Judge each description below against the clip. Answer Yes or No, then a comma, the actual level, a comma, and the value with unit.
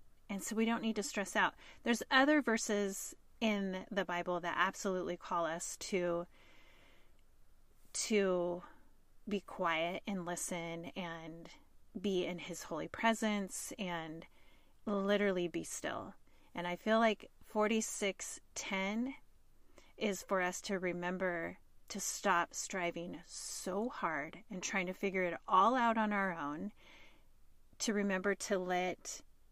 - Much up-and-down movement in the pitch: No, average, 3.4 semitones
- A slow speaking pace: Yes, slow, 130 wpm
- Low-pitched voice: No, high, 190 Hz